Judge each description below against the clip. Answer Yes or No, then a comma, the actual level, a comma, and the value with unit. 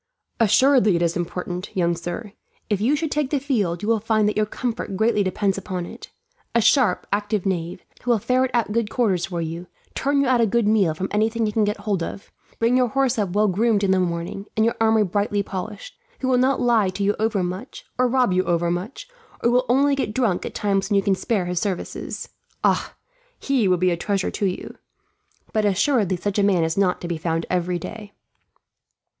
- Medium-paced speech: No, fast, 220 wpm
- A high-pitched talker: Yes, high, 205 Hz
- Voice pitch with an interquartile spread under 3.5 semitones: No, average, 4.2 semitones